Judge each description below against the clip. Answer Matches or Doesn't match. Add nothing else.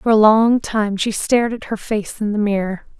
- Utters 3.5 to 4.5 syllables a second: Doesn't match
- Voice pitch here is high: Matches